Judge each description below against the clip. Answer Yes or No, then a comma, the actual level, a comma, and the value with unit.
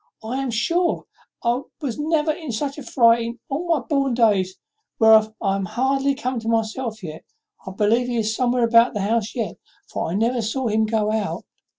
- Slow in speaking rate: No, average, 195 wpm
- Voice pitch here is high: Yes, high, 230 Hz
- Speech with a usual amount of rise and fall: Yes, average, 3.4 semitones